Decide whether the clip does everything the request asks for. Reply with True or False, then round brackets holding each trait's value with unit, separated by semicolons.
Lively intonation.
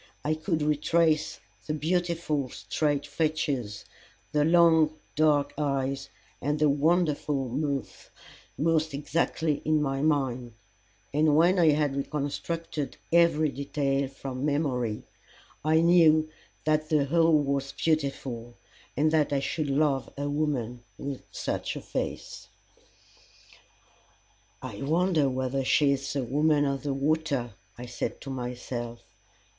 False (2.4 semitones)